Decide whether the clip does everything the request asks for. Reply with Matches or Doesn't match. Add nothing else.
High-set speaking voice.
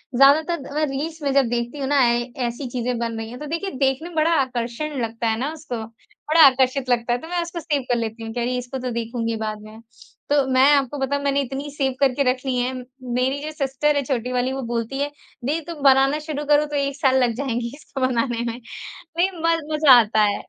Matches